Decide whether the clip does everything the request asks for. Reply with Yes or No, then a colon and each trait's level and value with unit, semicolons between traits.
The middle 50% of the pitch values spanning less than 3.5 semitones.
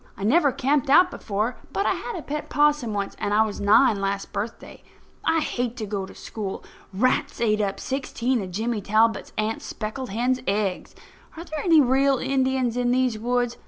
No: average, 4.1 semitones